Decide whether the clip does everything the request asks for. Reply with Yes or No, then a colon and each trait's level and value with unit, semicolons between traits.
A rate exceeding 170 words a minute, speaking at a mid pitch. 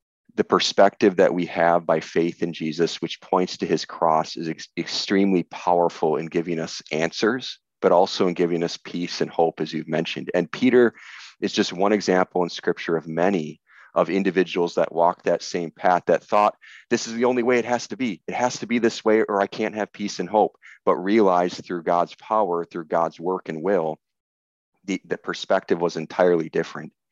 No: average, 200 wpm; very low, 90 Hz